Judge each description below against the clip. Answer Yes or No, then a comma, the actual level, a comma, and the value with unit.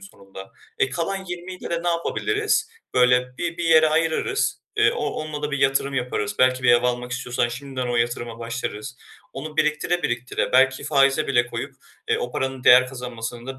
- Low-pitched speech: Yes, low, 130 Hz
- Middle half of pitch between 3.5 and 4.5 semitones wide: Yes, average, 4.2 semitones